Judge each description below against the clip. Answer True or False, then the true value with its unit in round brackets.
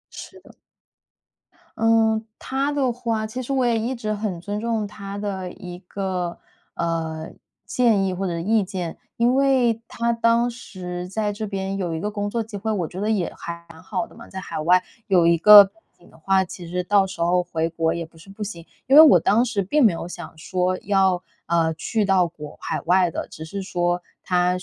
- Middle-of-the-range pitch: False (195 Hz)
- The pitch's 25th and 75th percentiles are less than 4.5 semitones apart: True (4.0 semitones)